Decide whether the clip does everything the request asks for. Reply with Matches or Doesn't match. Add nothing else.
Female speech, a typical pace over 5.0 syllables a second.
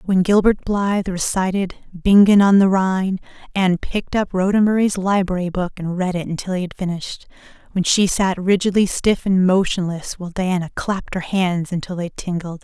Matches